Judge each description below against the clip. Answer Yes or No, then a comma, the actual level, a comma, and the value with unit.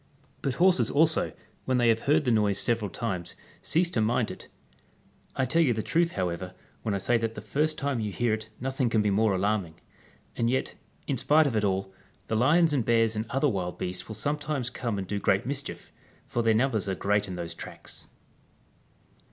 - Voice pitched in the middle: No, low, 115 Hz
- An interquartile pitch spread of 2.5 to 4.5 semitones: No, average, 4.9 semitones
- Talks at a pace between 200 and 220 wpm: Yes, fast, 205 wpm